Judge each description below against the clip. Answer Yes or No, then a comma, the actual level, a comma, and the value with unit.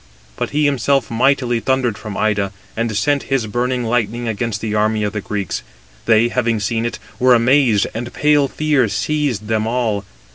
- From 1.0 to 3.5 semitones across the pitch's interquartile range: Yes, average, 3.1 semitones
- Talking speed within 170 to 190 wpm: Yes, average, 175 wpm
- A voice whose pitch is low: Yes, low, 115 Hz